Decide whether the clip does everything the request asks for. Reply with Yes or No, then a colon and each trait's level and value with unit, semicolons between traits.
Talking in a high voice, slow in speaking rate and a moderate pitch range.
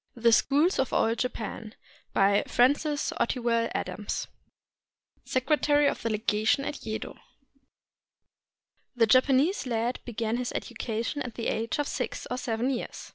Yes: high, 240 Hz; slow, 130 wpm; average, 3.3 semitones